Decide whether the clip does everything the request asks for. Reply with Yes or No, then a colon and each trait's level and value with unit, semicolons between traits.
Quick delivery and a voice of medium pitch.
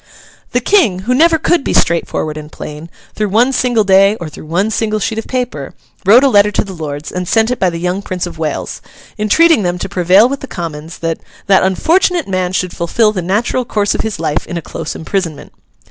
No: fast, 220 wpm; high, 195 Hz